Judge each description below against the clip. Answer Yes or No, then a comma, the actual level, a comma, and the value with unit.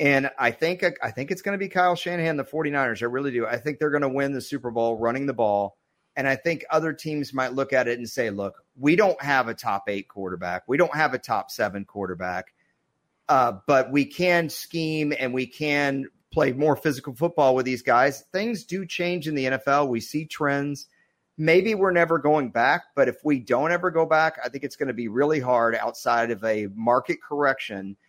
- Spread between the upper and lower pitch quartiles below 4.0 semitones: No, average, 4.8 semitones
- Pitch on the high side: No, medium, 140 Hz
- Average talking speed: No, fast, 220 wpm